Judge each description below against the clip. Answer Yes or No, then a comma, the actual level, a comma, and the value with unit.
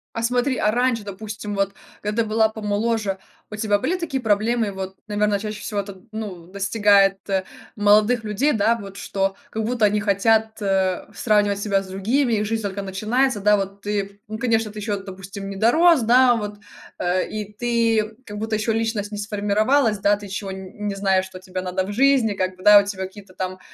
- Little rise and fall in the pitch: Yes, narrow, 2.1 semitones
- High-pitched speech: Yes, high, 210 Hz